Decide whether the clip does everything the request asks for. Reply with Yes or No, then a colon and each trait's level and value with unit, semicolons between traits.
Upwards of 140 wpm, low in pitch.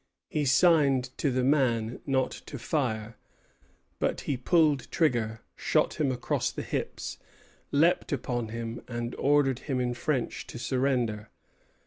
No: slow, 135 wpm; low, 130 Hz